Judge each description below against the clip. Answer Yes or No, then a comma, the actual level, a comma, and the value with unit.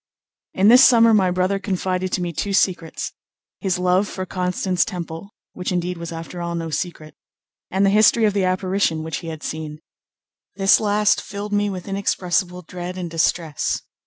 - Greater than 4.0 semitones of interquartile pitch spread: No, narrow, 2.4 semitones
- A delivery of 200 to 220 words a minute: No, average, 175 wpm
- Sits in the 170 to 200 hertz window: Yes, medium, 185 Hz